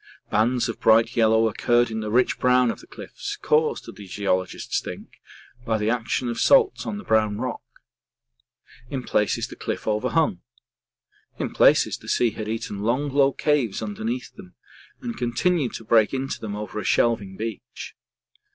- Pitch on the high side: No, low, 115 Hz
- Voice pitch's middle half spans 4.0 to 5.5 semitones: No, average, 2.8 semitones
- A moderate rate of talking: Yes, average, 170 wpm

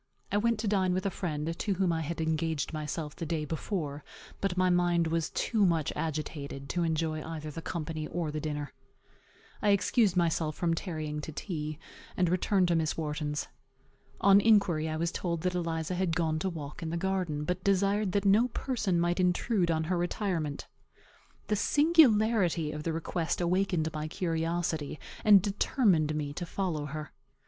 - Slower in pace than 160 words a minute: No, average, 175 wpm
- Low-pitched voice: No, medium, 170 Hz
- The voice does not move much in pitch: No, average, 3.3 semitones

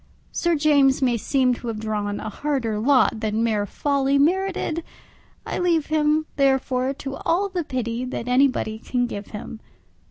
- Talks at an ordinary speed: Yes, average, 160 wpm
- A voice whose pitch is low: No, very high, 265 Hz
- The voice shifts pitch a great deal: No, average, 4.7 semitones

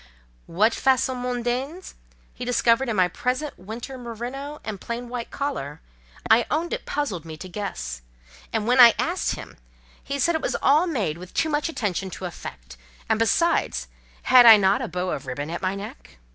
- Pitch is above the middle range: Yes, high, 230 Hz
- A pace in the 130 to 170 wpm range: No, average, 180 wpm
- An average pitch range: No, wide, 6.4 semitones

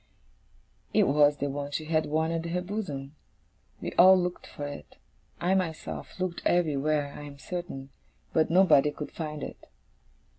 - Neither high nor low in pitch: Yes, medium, 155 Hz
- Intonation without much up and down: No, average, 3.4 semitones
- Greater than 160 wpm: No, average, 155 wpm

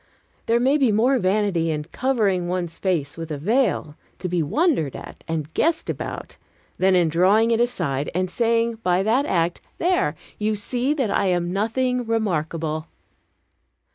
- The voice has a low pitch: No, high, 195 Hz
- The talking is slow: No, average, 160 wpm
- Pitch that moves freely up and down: Yes, wide, 6.0 semitones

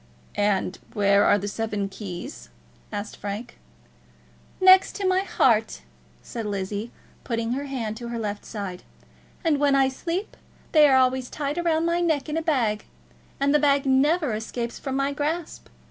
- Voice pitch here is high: Yes, very high, 260 Hz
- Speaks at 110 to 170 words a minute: Yes, average, 160 wpm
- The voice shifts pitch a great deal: Yes, wide, 6.0 semitones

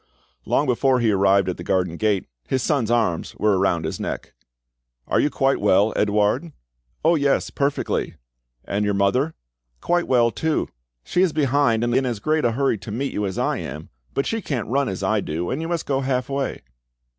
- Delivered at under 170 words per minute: No, average, 200 wpm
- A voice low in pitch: Yes, low, 120 Hz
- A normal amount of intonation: No, wide, 5.7 semitones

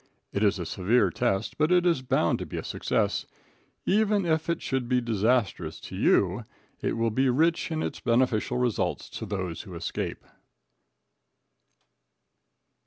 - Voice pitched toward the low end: Yes, low, 125 Hz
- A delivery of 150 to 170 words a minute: Yes, average, 155 wpm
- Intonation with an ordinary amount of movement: No, wide, 7.0 semitones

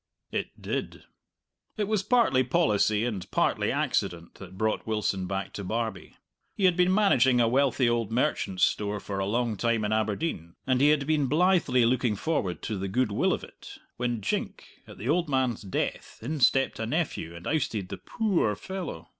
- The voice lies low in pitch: Yes, low, 120 Hz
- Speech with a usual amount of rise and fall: No, wide, 6.5 semitones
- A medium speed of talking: Yes, average, 185 wpm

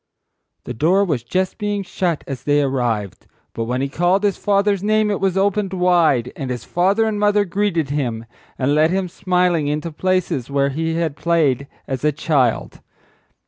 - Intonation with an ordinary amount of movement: No, wide, 5.9 semitones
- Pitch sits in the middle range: Yes, medium, 165 Hz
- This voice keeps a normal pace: Yes, average, 170 wpm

